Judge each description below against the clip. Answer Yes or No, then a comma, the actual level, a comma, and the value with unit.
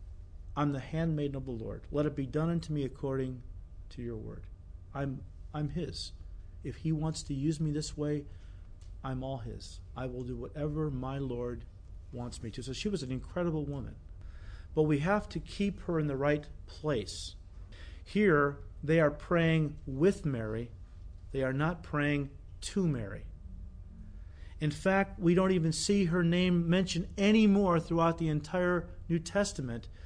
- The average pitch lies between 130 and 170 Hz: Yes, low, 135 Hz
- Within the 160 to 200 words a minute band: Yes, average, 165 wpm